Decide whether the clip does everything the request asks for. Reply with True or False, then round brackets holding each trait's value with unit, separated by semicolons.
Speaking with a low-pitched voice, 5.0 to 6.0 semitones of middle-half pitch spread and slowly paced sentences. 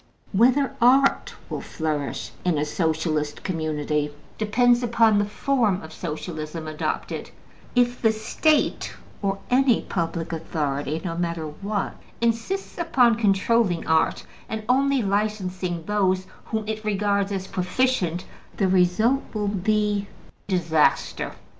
False (200 Hz; 5.6 semitones; 120 wpm)